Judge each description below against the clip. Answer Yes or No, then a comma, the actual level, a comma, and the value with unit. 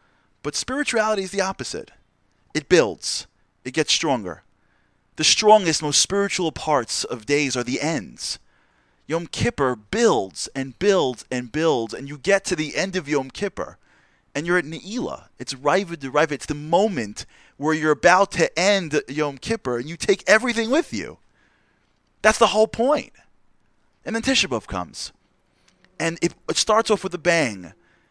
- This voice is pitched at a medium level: Yes, medium, 160 Hz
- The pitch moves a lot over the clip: Yes, wide, 6.4 semitones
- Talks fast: No, average, 160 wpm